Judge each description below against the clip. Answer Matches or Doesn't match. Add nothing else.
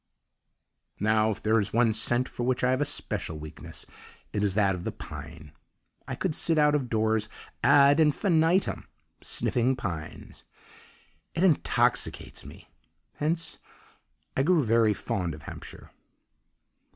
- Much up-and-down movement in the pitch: Matches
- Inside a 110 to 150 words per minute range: Matches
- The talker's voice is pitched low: Matches